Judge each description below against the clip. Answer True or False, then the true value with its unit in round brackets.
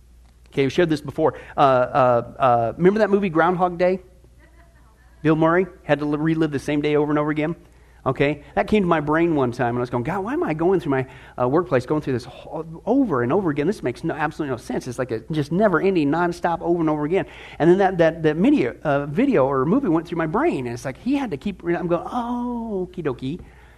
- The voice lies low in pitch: False (155 Hz)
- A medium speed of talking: False (240 wpm)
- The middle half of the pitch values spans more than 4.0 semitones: True (5.5 semitones)